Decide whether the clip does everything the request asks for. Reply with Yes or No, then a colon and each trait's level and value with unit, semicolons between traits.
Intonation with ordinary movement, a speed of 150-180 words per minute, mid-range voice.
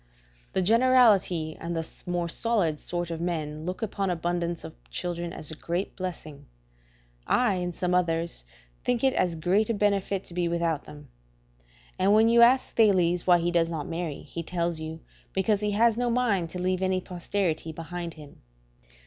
Yes: average, 3.2 semitones; average, 175 wpm; medium, 175 Hz